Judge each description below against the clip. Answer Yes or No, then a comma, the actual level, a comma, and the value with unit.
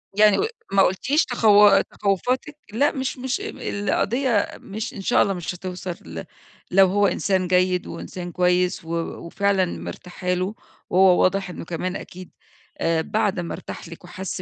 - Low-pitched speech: No, high, 190 Hz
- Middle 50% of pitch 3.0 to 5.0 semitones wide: No, narrow, 2.6 semitones